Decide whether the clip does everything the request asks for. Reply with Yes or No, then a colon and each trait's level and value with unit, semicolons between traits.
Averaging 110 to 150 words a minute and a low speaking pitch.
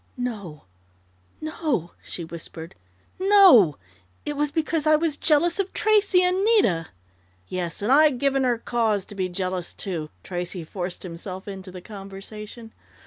No: average, 145 wpm; high, 210 Hz